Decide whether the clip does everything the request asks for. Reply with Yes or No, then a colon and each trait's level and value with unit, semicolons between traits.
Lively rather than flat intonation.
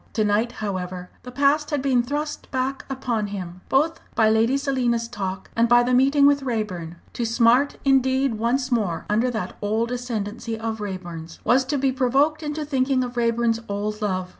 No: average, 4.1 semitones